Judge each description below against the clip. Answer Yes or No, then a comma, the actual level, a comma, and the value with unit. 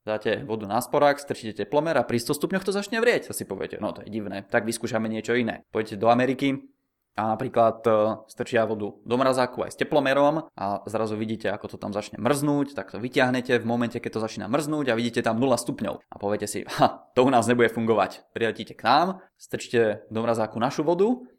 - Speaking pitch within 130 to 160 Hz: No, low, 115 Hz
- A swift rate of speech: Yes, fast, 210 wpm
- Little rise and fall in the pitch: No, average, 3.7 semitones